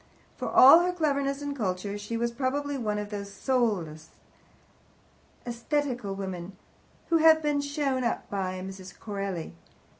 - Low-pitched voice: No, high, 235 Hz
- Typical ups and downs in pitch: No, wide, 6.4 semitones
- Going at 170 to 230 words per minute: No, average, 145 wpm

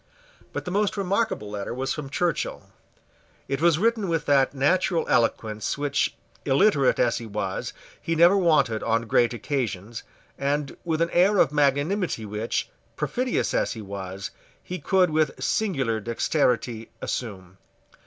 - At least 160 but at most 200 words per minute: No, average, 145 wpm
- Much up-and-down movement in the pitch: Yes, wide, 7.4 semitones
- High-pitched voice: No, medium, 140 Hz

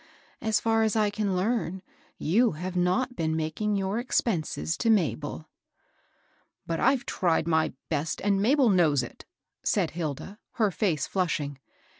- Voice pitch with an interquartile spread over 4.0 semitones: Yes, average, 5.3 semitones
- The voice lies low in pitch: No, medium, 185 Hz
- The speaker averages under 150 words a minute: No, average, 155 wpm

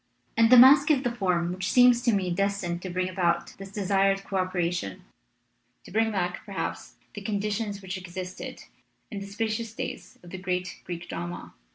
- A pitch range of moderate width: Yes, average, 3.0 semitones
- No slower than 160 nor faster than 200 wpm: Yes, average, 180 wpm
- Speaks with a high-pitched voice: Yes, high, 195 Hz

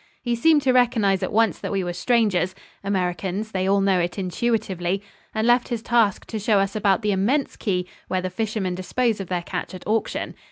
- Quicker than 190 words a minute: Yes, fast, 205 wpm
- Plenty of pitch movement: No, average, 3.5 semitones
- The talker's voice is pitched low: No, high, 200 Hz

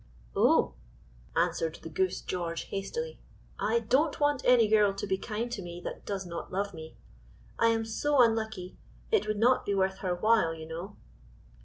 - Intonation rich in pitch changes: No, average, 4.1 semitones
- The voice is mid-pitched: No, high, 205 Hz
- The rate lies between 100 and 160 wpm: No, average, 175 wpm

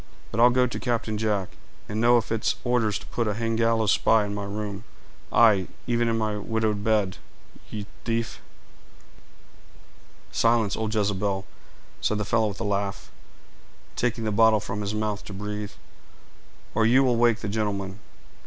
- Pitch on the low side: Yes, low, 110 Hz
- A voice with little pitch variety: Yes, narrow, 1.9 semitones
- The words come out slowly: No, average, 165 wpm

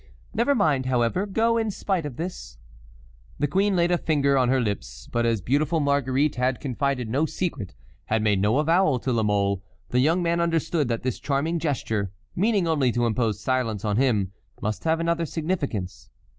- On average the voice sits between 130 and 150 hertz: Yes, medium, 140 Hz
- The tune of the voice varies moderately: No, wide, 6.4 semitones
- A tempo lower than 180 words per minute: No, average, 185 wpm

